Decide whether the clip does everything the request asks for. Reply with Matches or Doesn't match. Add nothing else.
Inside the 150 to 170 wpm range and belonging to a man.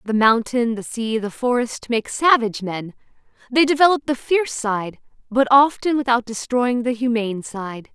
Doesn't match